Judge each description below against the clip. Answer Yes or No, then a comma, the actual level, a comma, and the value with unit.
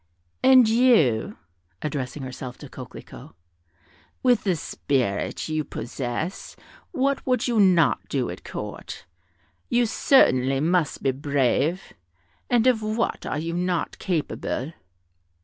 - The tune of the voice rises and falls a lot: Yes, wide, 9.0 semitones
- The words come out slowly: Yes, slow, 115 wpm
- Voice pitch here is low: No, medium, 170 Hz